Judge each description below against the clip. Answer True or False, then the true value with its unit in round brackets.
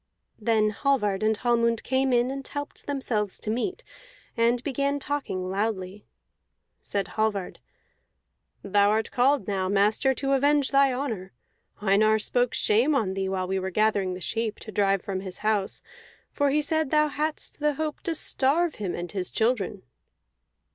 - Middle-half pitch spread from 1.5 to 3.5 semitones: False (5.5 semitones)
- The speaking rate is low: False (160 wpm)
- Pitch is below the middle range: False (225 Hz)